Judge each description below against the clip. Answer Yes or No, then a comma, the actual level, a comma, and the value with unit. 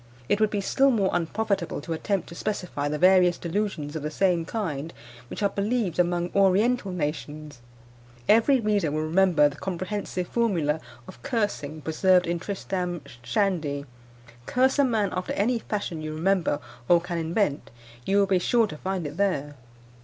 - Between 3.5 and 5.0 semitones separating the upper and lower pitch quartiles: Yes, average, 4.4 semitones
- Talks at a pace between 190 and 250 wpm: No, average, 165 wpm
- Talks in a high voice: No, medium, 180 Hz